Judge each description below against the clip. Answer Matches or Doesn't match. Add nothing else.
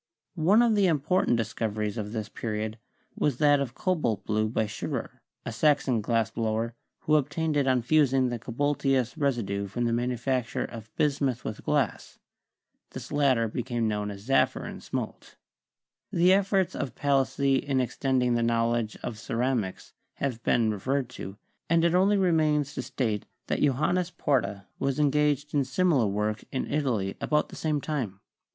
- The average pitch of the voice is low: Matches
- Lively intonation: Doesn't match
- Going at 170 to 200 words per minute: Doesn't match